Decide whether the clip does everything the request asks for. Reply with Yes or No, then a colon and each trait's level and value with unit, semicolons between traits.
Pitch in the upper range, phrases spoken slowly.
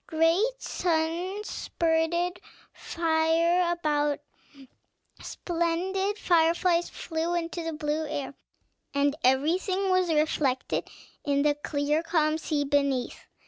Yes: very high, 325 Hz; slow, 100 wpm